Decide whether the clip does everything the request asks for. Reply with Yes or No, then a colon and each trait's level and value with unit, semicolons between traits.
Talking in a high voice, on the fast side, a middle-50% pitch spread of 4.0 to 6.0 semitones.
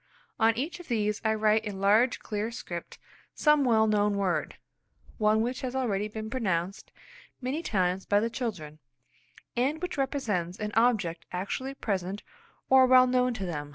No: high, 220 Hz; average, 160 wpm; average, 4.3 semitones